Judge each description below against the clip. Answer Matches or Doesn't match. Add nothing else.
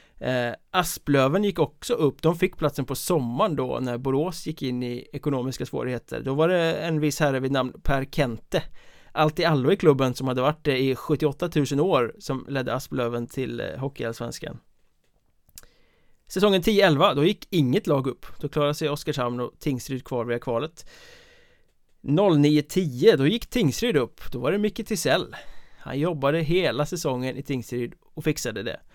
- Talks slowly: Doesn't match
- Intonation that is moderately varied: Matches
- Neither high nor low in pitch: Matches